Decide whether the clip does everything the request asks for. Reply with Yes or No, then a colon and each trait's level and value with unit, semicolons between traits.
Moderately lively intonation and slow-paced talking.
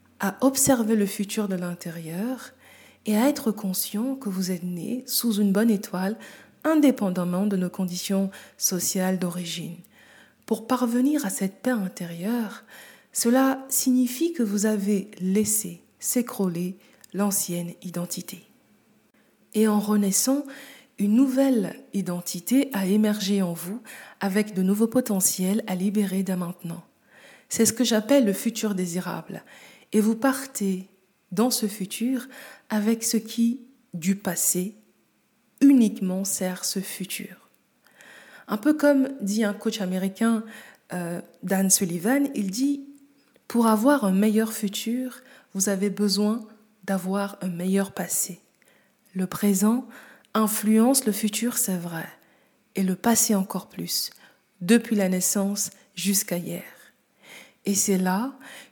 Yes: average, 4.4 semitones; slow, 125 wpm